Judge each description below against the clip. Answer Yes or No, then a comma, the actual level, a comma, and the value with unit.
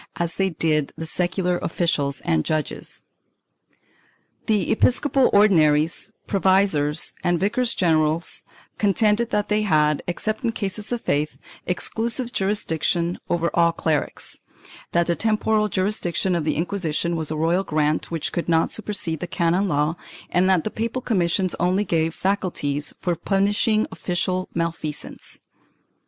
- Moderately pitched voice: Yes, medium, 175 Hz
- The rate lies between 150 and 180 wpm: No, slow, 135 wpm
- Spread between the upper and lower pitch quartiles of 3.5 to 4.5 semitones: Yes, average, 4.1 semitones